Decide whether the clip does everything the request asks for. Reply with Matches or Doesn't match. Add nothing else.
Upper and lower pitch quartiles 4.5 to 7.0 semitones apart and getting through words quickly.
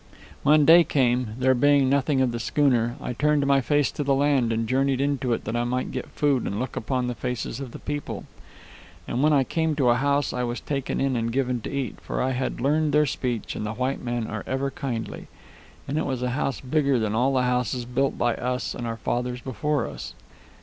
Doesn't match